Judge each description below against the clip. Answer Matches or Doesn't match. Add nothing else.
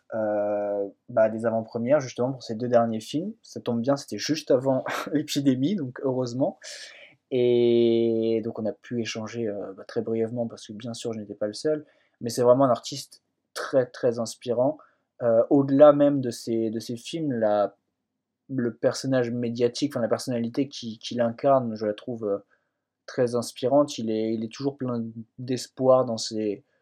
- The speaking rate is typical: Matches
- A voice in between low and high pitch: Doesn't match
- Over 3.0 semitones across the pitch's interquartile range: Doesn't match